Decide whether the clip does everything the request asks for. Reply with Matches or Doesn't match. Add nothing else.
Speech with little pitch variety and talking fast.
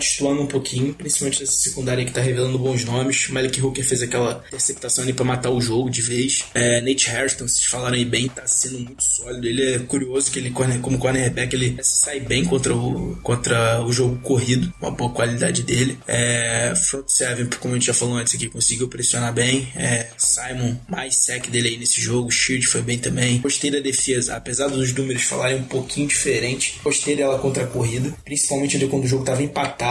Matches